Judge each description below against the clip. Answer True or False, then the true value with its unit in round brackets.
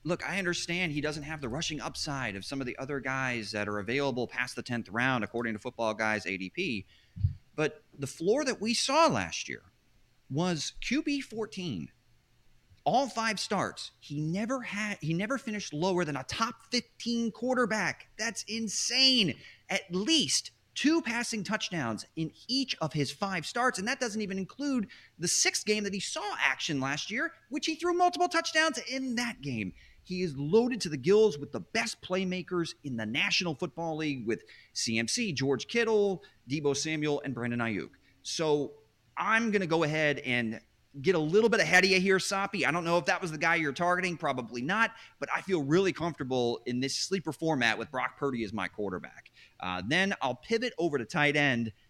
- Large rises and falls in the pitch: True (8.5 semitones)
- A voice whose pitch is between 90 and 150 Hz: False (170 Hz)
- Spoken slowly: False (185 wpm)